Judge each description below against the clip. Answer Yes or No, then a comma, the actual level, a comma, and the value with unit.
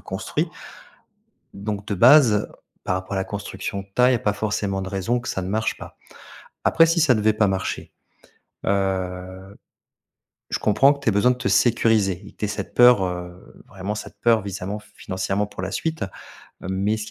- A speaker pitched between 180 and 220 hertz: No, low, 100 Hz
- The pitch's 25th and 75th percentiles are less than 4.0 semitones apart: Yes, average, 2.7 semitones